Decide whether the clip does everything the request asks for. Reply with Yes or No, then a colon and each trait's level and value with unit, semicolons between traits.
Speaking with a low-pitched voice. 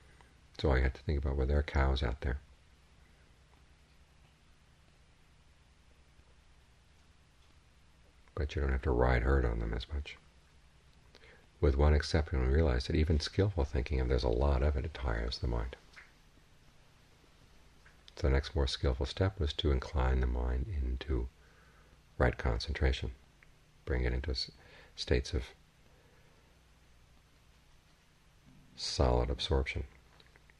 Yes: very low, 75 Hz